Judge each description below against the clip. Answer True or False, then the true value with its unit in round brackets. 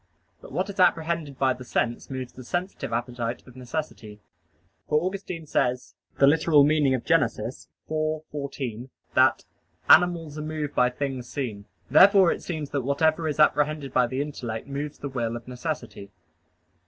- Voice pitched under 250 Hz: True (140 Hz)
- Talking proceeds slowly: False (155 wpm)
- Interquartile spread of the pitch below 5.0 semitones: True (3.9 semitones)